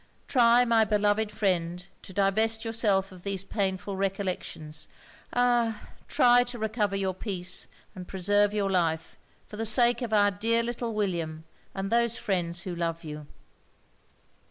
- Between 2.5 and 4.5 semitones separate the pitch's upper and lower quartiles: Yes, average, 3.4 semitones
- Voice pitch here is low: No, high, 200 Hz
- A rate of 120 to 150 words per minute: Yes, average, 145 wpm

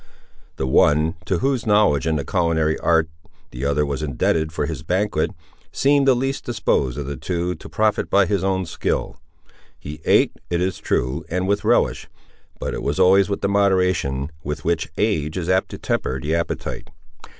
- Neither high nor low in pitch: No, very low, 85 Hz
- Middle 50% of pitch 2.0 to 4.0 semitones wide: No, average, 4.8 semitones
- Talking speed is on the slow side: No, average, 185 wpm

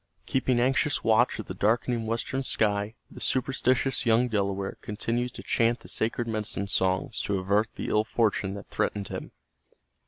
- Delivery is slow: No, average, 160 wpm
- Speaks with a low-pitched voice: Yes, low, 110 Hz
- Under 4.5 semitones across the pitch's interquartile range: Yes, average, 3.1 semitones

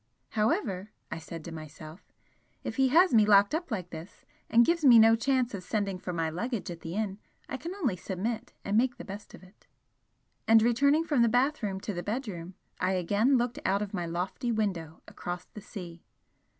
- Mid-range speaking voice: No, high, 210 Hz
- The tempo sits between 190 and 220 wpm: Yes, average, 200 wpm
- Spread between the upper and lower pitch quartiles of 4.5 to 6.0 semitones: Yes, average, 5.2 semitones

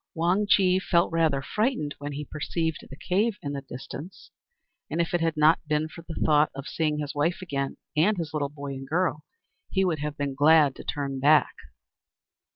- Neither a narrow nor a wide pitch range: Yes, average, 3.0 semitones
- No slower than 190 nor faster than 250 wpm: Yes, average, 195 wpm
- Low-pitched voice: No, medium, 155 Hz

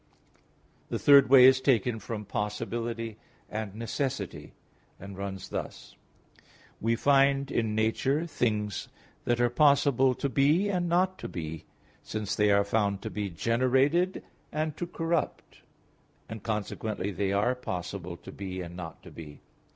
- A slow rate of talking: No, average, 145 wpm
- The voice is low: Yes, low, 115 Hz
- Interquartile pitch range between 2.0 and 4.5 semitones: No, wide, 5.4 semitones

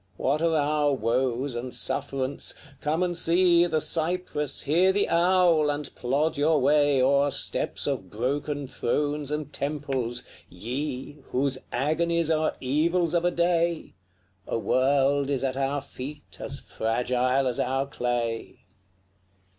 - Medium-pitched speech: Yes, medium, 145 Hz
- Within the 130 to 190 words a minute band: Yes, slow, 135 wpm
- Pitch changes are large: No, average, 3.4 semitones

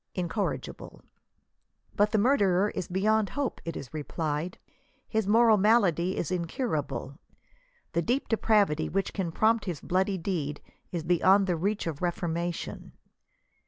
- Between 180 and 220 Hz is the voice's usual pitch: Yes, medium, 185 Hz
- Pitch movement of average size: Yes, average, 4.0 semitones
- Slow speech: Yes, slow, 130 wpm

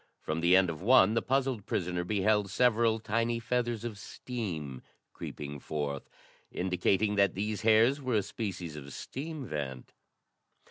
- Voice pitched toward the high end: No, low, 105 Hz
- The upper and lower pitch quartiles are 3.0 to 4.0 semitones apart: No, average, 5.0 semitones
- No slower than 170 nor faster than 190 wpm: No, average, 145 wpm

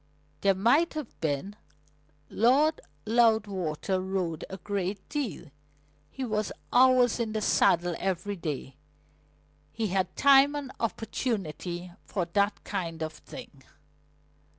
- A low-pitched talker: No, high, 200 Hz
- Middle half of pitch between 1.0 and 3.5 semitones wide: No, average, 5.1 semitones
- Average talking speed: No, slow, 115 wpm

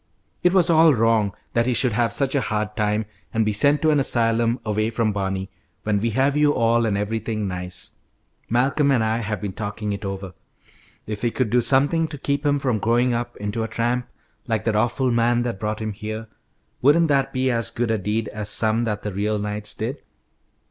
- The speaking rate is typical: No, fast, 210 wpm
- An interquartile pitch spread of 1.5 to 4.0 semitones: Yes, average, 3.0 semitones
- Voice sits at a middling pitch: No, low, 115 Hz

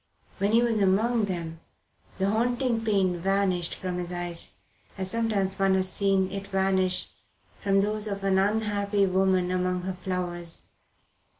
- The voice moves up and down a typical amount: No, narrow, 1.9 semitones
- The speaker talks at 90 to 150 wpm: Yes, average, 145 wpm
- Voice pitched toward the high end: Yes, high, 195 Hz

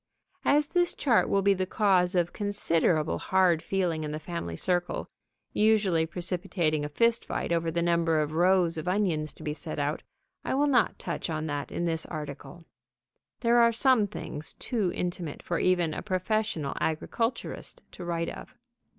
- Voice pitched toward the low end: No, medium, 175 Hz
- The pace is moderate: Yes, average, 170 wpm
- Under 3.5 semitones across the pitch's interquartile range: No, average, 4.2 semitones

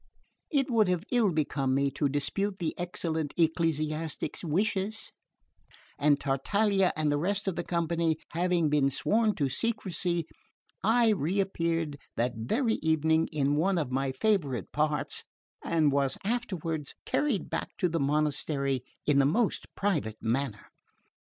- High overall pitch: No, medium, 160 Hz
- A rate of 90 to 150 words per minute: Yes, average, 140 wpm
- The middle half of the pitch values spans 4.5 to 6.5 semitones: Yes, average, 5.1 semitones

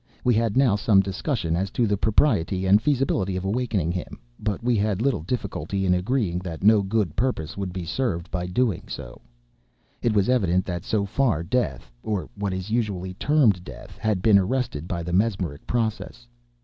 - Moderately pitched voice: No, low, 100 Hz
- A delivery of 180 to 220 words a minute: Yes, average, 185 wpm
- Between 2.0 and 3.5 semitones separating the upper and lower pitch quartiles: No, average, 4.2 semitones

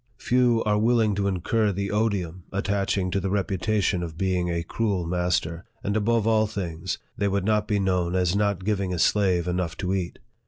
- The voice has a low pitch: Yes, very low, 95 Hz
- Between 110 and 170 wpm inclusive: No, average, 190 wpm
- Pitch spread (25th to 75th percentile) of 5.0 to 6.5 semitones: No, average, 2.7 semitones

